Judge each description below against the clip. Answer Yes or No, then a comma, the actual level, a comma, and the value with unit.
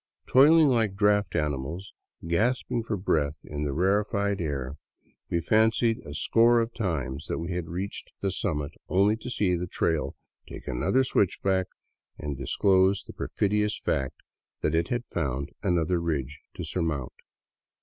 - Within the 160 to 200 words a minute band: No, average, 150 wpm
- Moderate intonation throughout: No, wide, 5.7 semitones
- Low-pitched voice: Yes, very low, 90 Hz